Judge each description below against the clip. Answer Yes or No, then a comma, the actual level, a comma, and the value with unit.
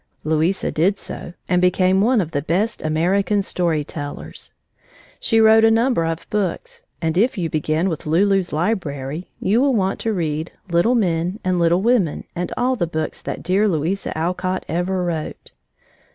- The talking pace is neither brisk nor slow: Yes, average, 165 wpm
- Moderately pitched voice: Yes, medium, 180 Hz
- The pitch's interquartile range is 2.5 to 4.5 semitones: Yes, average, 4.1 semitones